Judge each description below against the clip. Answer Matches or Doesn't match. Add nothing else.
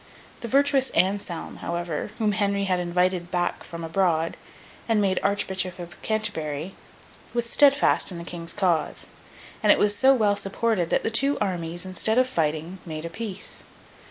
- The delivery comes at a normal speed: Matches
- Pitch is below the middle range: Doesn't match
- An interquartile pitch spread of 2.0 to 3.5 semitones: Doesn't match